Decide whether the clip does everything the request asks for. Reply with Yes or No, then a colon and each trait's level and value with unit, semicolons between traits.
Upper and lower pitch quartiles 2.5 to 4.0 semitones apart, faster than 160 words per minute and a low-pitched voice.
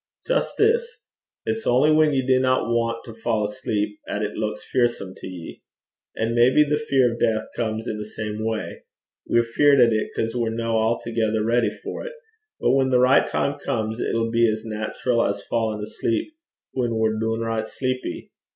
Yes: average, 2.8 semitones; average, 180 wpm; low, 115 Hz